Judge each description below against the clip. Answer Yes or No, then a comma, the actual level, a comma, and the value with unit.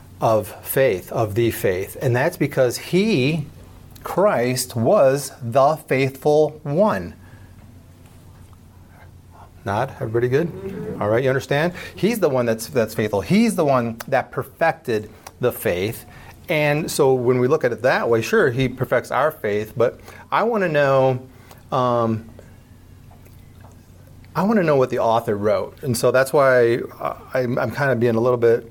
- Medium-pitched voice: No, low, 125 Hz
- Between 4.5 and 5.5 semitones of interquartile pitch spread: No, average, 3.9 semitones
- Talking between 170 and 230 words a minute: No, average, 155 wpm